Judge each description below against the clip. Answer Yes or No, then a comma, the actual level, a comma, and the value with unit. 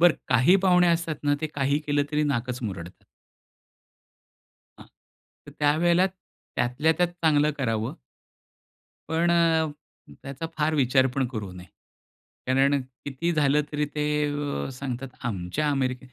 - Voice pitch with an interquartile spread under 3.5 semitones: No, average, 3.9 semitones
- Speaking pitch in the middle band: Yes, medium, 145 Hz